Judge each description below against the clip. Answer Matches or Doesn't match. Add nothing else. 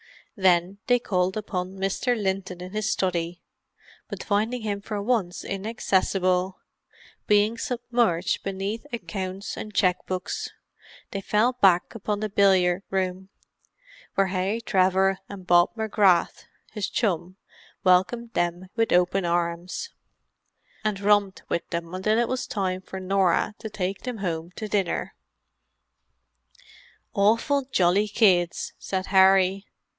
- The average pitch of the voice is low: Doesn't match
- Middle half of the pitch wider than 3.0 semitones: Doesn't match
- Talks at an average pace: Doesn't match